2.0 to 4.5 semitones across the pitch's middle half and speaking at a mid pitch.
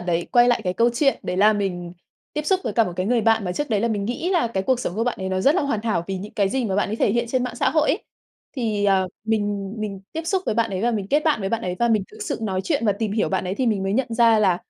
No: average, 3.8 semitones; high, 220 Hz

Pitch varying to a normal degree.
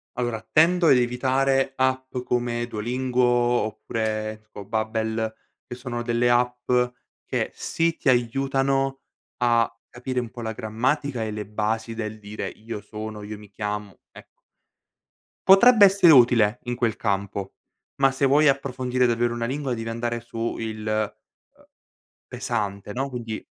Yes: average, 3.1 semitones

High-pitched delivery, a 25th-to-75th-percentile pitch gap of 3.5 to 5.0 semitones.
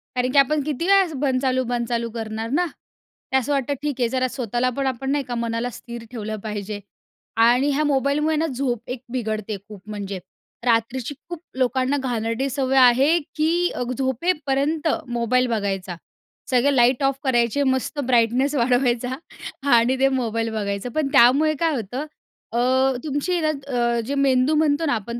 No: very high, 255 Hz; average, 3.1 semitones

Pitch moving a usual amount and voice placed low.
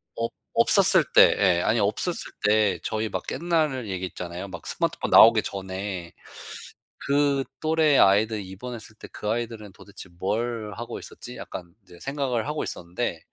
Yes: average, 4.7 semitones; low, 110 Hz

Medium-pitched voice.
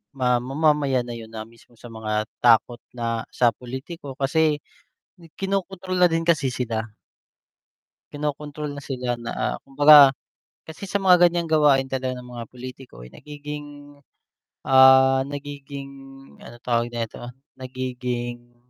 No: low, 130 Hz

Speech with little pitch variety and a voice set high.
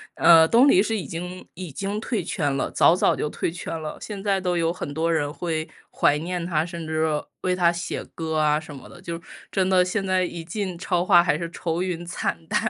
No: narrow, 2.3 semitones; medium, 170 Hz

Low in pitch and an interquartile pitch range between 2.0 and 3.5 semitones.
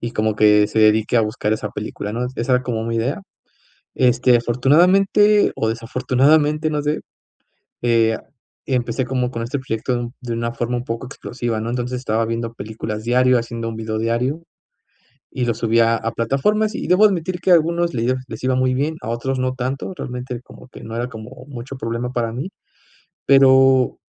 Yes: low, 125 Hz; narrow, 2.6 semitones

